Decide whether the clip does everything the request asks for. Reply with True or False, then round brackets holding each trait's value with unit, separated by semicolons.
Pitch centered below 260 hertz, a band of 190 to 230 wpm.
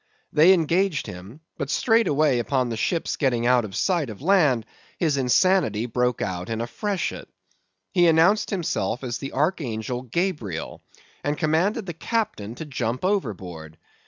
False (140 Hz; 150 wpm)